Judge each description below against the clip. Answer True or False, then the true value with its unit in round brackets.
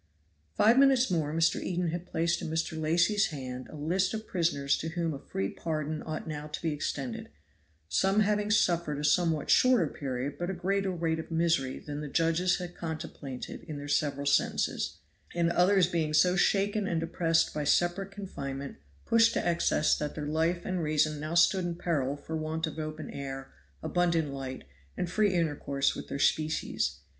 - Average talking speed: True (180 wpm)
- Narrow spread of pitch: False (3.1 semitones)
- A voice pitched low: False (160 Hz)